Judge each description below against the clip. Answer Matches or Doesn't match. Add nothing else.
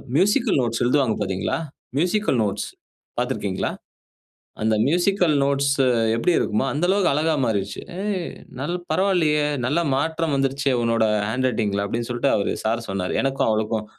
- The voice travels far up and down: Matches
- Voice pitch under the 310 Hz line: Matches